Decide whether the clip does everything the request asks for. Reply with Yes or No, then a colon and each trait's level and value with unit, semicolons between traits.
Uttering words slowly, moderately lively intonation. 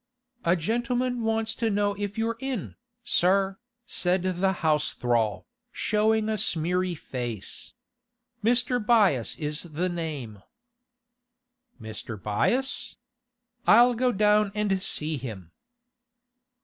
No: slow, 110 wpm; wide, 6.6 semitones